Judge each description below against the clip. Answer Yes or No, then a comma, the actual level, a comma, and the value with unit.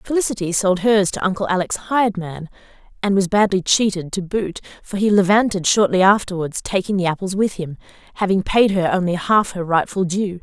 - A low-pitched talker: No, high, 190 Hz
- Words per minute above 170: Yes, average, 180 wpm